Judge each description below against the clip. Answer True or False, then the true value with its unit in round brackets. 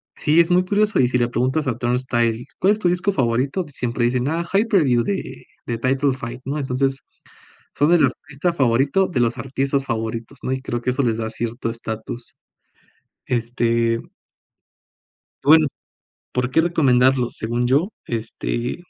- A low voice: True (130 Hz)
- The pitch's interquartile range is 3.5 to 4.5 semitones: True (3.8 semitones)